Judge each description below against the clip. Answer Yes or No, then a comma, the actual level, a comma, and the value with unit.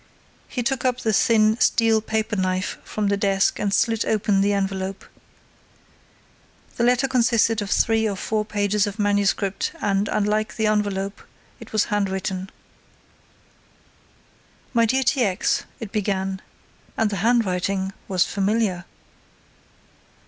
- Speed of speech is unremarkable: No, slow, 130 wpm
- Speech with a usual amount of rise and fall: No, narrow, 2.3 semitones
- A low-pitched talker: No, high, 210 Hz